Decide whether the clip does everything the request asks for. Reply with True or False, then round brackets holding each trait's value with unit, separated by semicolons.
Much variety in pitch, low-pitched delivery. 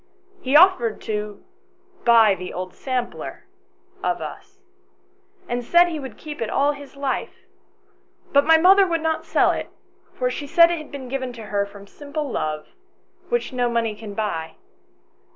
False (6.4 semitones; 260 Hz)